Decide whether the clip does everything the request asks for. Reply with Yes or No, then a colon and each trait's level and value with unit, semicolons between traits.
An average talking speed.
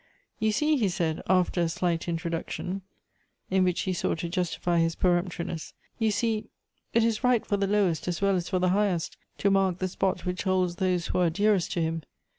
No: fast, 215 wpm